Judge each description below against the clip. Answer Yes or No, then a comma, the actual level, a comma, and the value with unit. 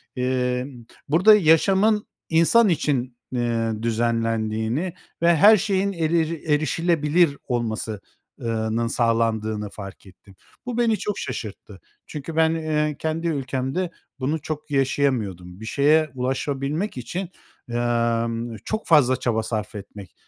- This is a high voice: No, low, 135 Hz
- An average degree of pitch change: No, wide, 6.0 semitones